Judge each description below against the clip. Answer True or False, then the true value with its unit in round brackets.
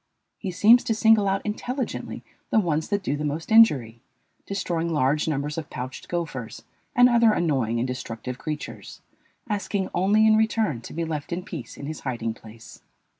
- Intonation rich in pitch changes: True (7.7 semitones)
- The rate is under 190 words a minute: True (175 wpm)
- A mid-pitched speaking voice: True (165 Hz)